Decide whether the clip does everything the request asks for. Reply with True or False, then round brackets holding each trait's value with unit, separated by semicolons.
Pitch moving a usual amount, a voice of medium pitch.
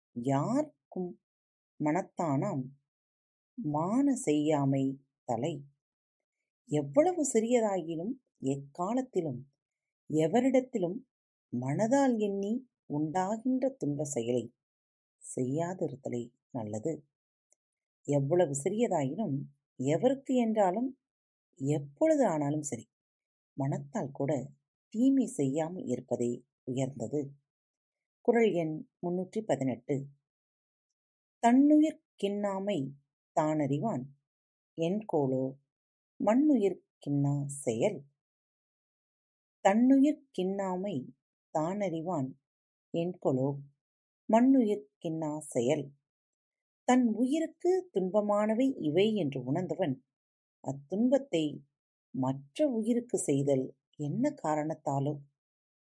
False (7.7 semitones; 155 Hz)